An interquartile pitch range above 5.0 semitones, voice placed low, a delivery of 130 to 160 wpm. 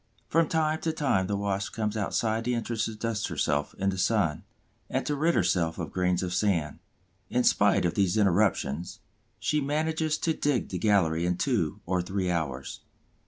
No: wide, 5.5 semitones; low, 100 Hz; average, 180 wpm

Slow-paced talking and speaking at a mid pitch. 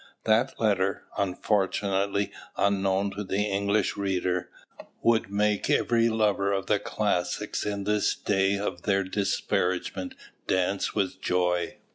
No: slow, 120 wpm; low, 100 Hz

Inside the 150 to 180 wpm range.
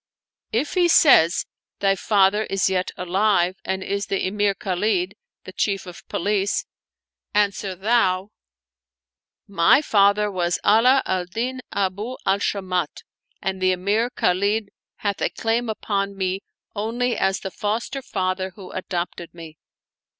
No: slow, 135 wpm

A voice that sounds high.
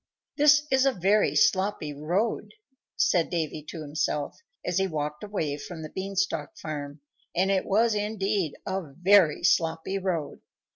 No: medium, 180 Hz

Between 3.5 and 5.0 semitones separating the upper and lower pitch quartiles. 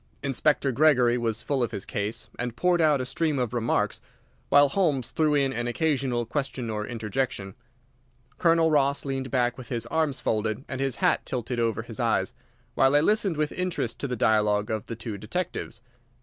Yes: average, 4.1 semitones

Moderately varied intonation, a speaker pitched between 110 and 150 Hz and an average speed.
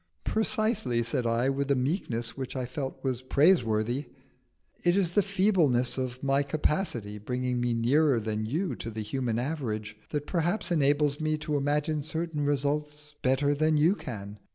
Yes: average, 4.3 semitones; medium, 140 Hz; average, 160 wpm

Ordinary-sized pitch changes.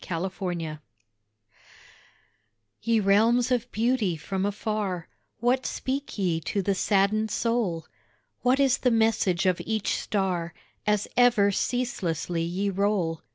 Yes: average, 4.2 semitones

